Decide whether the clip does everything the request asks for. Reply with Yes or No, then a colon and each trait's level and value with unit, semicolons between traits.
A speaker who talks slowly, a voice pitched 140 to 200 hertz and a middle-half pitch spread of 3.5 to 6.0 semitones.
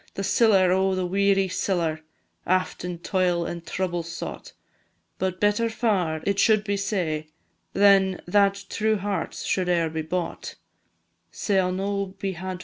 No: slow, 130 wpm; medium, 185 Hz; narrow, 2.4 semitones